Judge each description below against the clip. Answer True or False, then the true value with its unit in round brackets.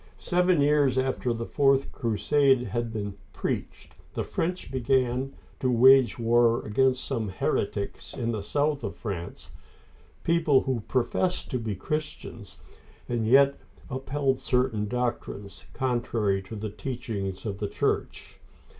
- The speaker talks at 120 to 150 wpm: True (135 wpm)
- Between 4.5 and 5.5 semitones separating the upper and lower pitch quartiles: False (3.8 semitones)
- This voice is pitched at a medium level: False (125 Hz)